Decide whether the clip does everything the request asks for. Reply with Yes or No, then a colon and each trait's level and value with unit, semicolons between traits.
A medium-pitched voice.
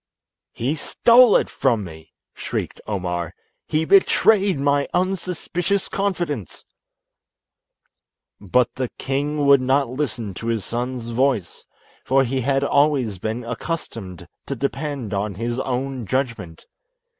No: low, 130 Hz